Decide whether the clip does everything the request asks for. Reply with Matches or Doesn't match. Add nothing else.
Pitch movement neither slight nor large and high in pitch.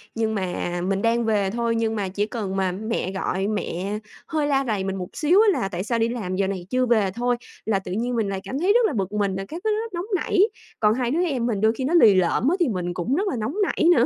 Matches